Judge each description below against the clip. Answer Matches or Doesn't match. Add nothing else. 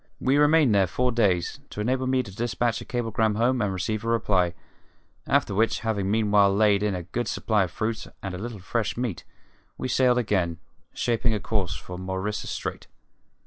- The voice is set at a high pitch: Doesn't match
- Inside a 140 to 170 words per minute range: Doesn't match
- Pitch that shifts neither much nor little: Matches